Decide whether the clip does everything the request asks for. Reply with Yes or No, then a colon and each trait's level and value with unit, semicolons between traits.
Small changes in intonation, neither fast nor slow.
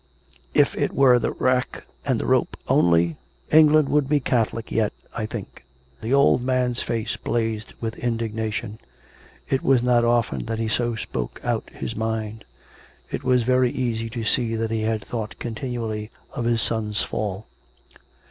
Yes: narrow, 2.2 semitones; average, 160 wpm